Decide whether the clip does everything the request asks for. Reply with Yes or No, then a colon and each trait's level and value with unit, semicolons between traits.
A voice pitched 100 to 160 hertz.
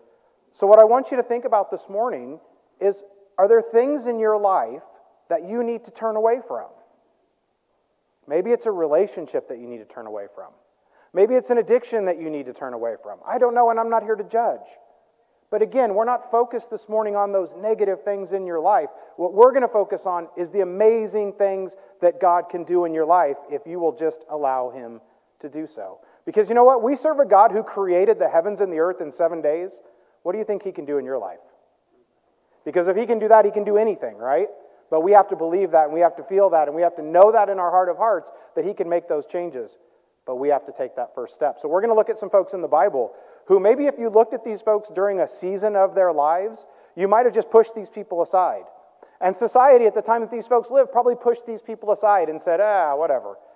No: high, 210 Hz